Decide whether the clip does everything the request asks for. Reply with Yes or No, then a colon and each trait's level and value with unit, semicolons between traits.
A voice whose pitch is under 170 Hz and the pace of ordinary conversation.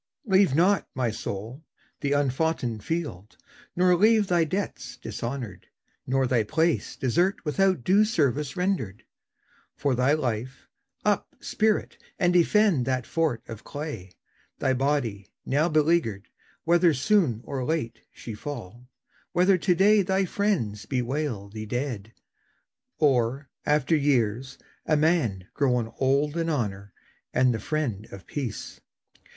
No: medium, 140 Hz; slow, 130 wpm